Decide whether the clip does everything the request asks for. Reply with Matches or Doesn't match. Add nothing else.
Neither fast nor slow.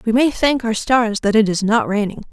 Doesn't match